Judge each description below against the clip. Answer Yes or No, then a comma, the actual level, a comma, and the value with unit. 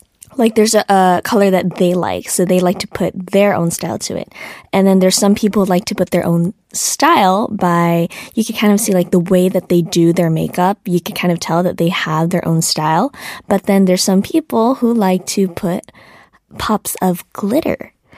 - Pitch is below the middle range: No, medium, 185 Hz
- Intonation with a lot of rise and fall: No, narrow, 2.4 semitones